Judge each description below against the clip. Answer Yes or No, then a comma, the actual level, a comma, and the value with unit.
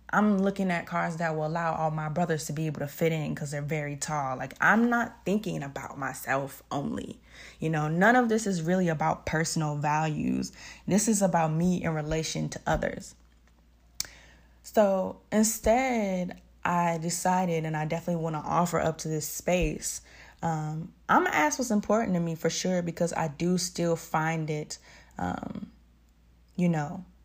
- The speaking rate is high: No, average, 170 wpm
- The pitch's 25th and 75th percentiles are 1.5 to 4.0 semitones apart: Yes, average, 3.3 semitones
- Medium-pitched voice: Yes, medium, 165 Hz